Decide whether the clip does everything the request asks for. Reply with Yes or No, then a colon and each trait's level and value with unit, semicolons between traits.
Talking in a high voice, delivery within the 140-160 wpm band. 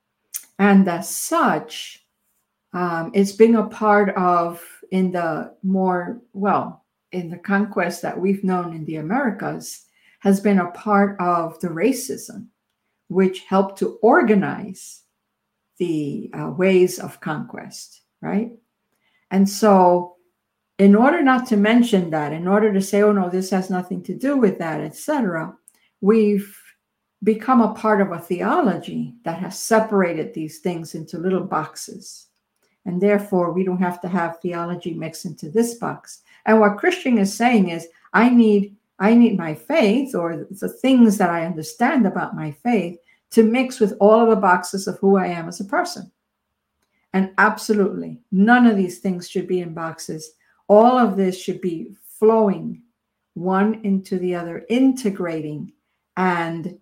Yes: high, 195 Hz; average, 155 wpm